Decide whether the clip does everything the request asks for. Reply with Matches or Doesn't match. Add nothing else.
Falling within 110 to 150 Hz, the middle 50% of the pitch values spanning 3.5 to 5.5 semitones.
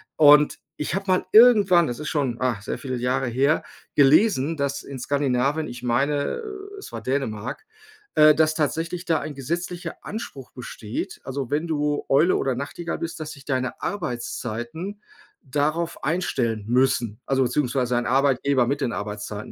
Matches